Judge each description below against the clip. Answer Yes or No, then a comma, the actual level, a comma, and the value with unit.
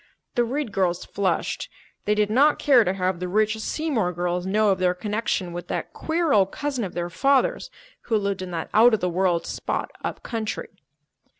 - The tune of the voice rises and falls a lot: No, average, 4.7 semitones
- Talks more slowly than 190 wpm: No, average, 195 wpm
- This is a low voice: No, high, 205 Hz